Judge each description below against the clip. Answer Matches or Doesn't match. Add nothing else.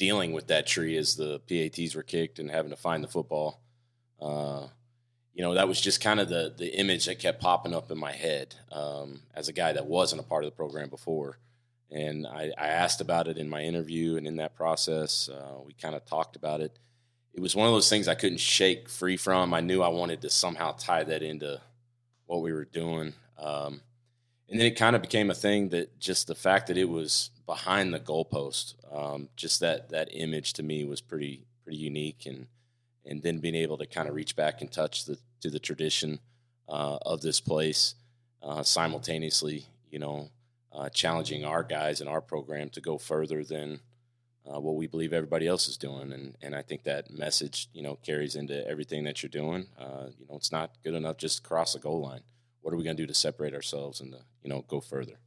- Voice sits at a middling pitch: Doesn't match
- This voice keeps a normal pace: Doesn't match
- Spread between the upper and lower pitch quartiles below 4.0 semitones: Doesn't match